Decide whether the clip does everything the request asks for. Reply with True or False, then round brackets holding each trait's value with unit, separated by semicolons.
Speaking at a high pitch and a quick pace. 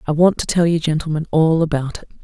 False (160 Hz; 240 wpm)